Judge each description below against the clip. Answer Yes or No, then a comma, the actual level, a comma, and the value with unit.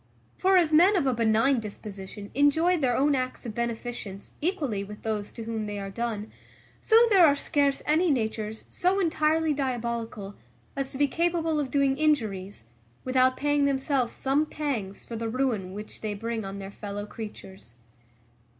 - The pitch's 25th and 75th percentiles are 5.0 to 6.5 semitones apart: Yes, wide, 5.5 semitones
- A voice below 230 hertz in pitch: No, very high, 250 Hz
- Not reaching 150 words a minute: No, average, 170 wpm